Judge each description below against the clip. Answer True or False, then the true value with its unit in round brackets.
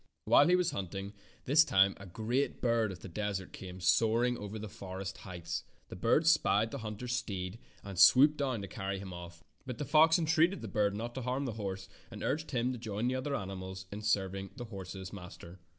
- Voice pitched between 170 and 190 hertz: False (105 Hz)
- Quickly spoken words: True (210 wpm)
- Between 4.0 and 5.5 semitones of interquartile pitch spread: True (4.7 semitones)